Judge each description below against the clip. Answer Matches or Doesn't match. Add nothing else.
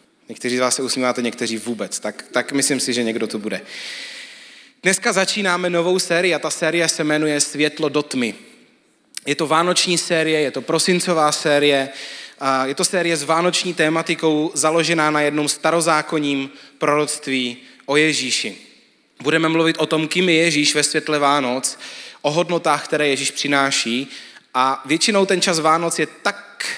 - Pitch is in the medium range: Matches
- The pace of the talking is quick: Doesn't match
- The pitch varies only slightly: Doesn't match